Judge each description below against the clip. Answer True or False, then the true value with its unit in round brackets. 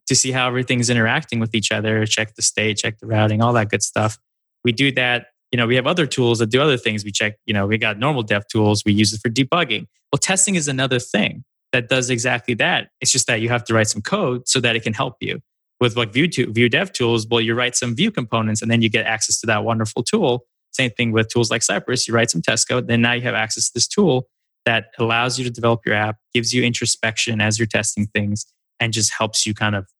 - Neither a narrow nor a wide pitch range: False (2.3 semitones)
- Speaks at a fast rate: True (260 wpm)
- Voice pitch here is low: True (115 Hz)